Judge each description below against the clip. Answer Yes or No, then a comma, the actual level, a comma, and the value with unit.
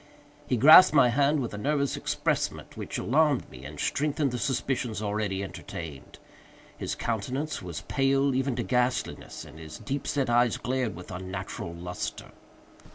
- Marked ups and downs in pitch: Yes, wide, 6.5 semitones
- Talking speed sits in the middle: Yes, average, 155 wpm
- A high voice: No, low, 125 Hz